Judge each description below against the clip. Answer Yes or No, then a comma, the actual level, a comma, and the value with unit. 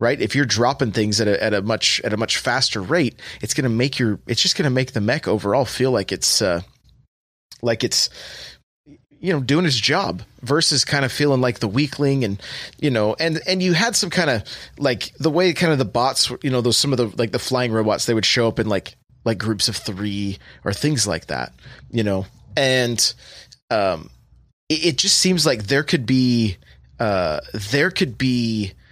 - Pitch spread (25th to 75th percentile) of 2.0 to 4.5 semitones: No, average, 5.2 semitones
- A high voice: No, low, 125 Hz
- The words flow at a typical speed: No, fast, 215 wpm